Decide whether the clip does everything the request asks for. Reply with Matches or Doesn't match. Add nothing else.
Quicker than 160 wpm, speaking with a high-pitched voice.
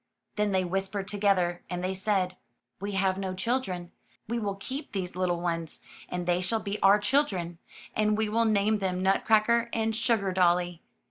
Matches